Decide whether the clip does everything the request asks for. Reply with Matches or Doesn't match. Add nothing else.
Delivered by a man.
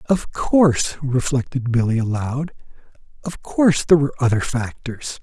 Matches